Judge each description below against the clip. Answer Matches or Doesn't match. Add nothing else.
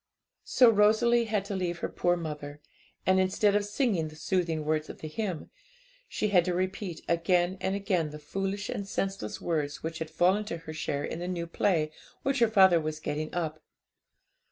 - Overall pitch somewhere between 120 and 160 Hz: Doesn't match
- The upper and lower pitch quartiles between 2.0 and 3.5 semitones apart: Doesn't match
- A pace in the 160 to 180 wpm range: Doesn't match